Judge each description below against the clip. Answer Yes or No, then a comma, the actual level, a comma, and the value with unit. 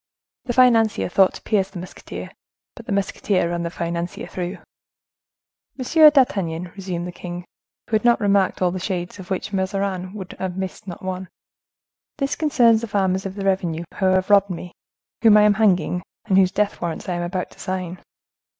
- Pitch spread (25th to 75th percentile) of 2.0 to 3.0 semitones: Yes, average, 2.7 semitones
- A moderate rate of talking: Yes, average, 185 wpm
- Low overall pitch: No, high, 190 Hz